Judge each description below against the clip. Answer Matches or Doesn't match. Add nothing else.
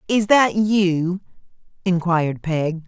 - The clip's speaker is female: Matches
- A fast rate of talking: Doesn't match